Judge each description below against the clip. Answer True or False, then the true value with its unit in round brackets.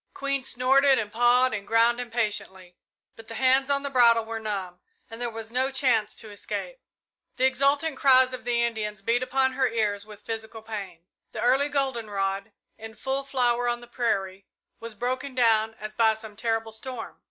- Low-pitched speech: False (235 Hz)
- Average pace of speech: True (180 wpm)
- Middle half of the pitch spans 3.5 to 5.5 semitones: False (3.0 semitones)